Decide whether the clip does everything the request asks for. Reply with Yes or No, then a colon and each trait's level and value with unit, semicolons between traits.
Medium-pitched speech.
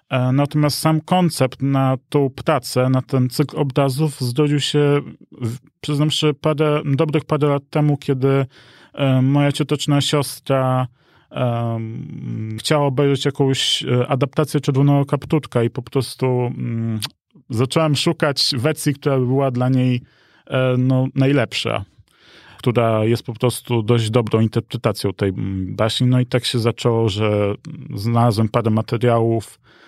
No: low, 130 Hz